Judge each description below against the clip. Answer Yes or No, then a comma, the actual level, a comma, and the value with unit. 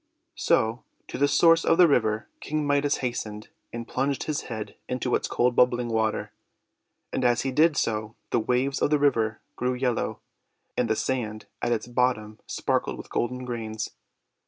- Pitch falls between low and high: No, low, 125 Hz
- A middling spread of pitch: Yes, average, 3.6 semitones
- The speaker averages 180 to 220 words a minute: No, average, 170 wpm